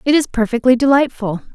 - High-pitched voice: Yes, very high, 250 Hz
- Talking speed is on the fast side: No, average, 155 wpm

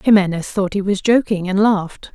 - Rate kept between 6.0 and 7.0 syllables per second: No, 5.2 syllables/s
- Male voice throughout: No, female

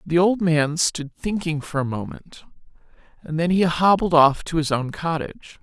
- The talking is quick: No, average, 180 wpm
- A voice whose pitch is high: No, medium, 165 Hz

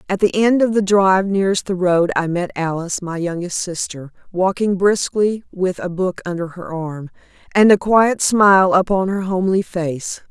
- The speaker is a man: No, female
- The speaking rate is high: No, average, 180 wpm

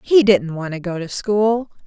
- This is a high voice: Yes, high, 200 Hz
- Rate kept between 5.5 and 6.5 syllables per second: No, 4.3 syllables/s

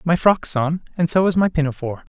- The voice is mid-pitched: Yes, medium, 155 Hz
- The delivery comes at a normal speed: No, fast, 225 wpm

